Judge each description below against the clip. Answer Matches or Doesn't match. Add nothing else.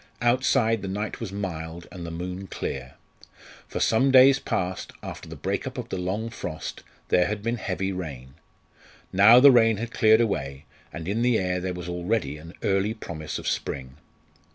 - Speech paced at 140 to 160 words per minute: Doesn't match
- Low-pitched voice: Matches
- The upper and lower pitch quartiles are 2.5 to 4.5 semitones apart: Doesn't match